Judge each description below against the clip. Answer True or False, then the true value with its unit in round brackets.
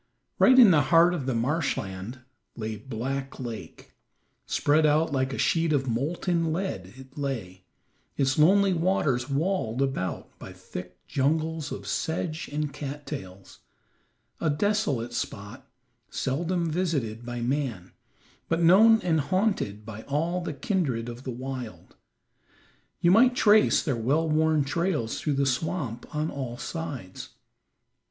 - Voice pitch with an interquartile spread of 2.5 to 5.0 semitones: False (5.5 semitones)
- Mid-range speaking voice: True (145 Hz)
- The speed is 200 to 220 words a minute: False (135 wpm)